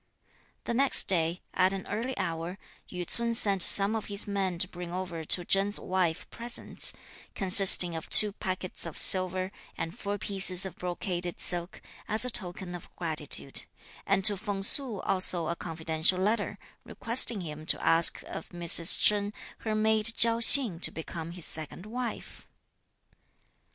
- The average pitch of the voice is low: No, medium, 185 Hz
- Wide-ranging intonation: No, average, 3.3 semitones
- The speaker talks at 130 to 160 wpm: Yes, average, 155 wpm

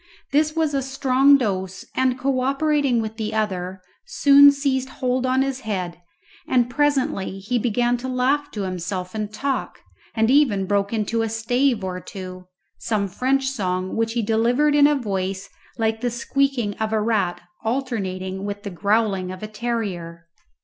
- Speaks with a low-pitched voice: No, high, 225 Hz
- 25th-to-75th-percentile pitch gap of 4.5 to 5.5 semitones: Yes, average, 5.1 semitones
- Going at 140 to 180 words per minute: Yes, average, 165 wpm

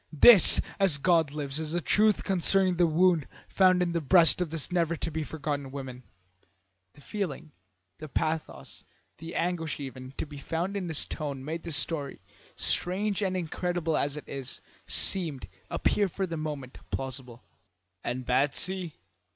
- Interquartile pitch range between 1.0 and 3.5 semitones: No, average, 4.1 semitones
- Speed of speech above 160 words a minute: No, average, 155 wpm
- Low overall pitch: No, medium, 160 Hz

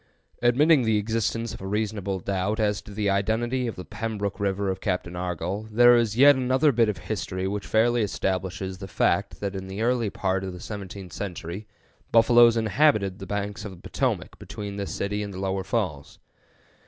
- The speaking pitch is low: Yes, low, 105 Hz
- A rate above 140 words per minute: Yes, average, 190 wpm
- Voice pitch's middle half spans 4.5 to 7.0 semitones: No, average, 2.9 semitones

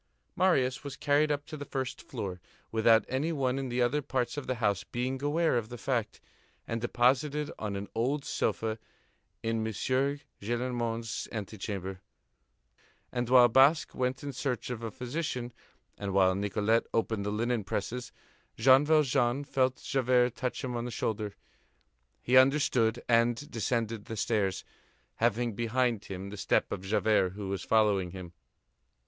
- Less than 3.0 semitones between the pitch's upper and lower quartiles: No, average, 3.3 semitones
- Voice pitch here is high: No, low, 120 Hz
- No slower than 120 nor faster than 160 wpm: Yes, average, 155 wpm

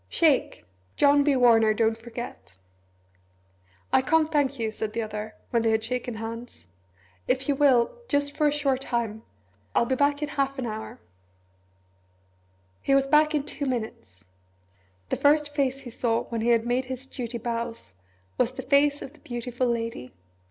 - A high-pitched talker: Yes, high, 245 Hz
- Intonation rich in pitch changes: No, average, 3.8 semitones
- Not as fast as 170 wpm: No, average, 175 wpm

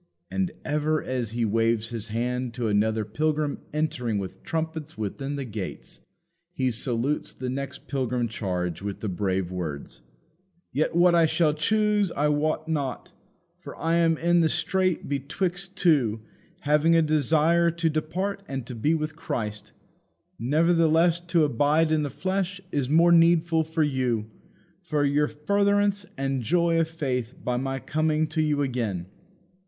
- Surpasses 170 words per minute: No, average, 155 wpm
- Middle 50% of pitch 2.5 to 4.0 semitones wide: No, average, 5.2 semitones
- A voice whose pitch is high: No, medium, 150 Hz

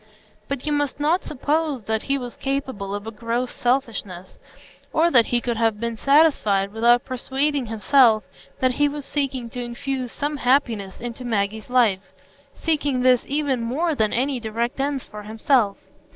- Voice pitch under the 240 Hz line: No, very high, 250 Hz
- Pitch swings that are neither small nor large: Yes, average, 3.9 semitones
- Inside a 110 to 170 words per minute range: Yes, average, 160 wpm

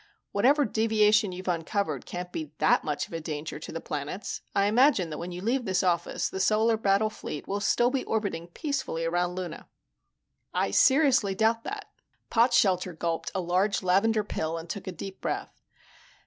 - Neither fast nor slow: Yes, average, 175 wpm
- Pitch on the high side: Yes, high, 195 Hz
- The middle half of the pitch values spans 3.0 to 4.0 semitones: No, average, 4.5 semitones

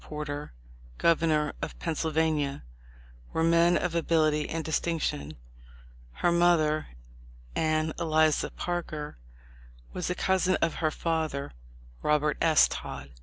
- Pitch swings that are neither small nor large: No, narrow, 1.8 semitones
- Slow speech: Yes, slow, 115 wpm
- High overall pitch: No, medium, 160 Hz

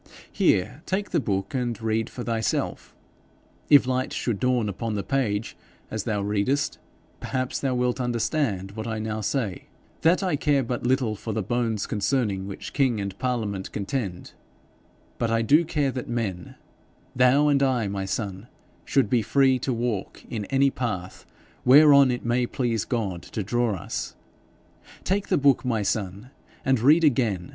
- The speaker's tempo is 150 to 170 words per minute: Yes, average, 165 wpm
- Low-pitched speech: Yes, low, 120 Hz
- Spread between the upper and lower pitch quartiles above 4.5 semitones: No, average, 4.1 semitones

